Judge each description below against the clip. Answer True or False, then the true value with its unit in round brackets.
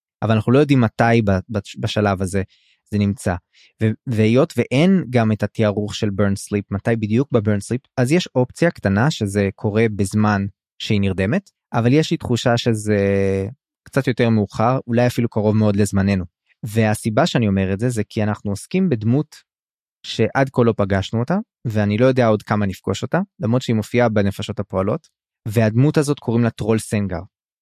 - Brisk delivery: True (165 wpm)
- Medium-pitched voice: False (110 Hz)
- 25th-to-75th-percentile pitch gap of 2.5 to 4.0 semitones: True (3.4 semitones)